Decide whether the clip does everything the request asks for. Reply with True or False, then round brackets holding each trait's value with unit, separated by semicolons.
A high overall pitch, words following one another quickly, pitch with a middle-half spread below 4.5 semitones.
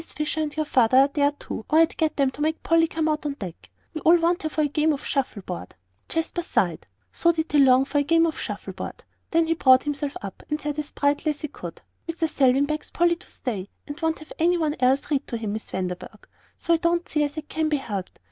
True (300 Hz; 255 wpm; 3.0 semitones)